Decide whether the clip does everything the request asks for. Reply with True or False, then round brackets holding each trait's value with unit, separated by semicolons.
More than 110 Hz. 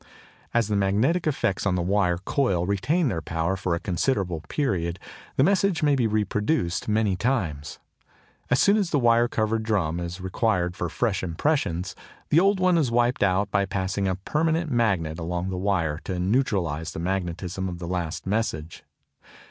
False (100 Hz)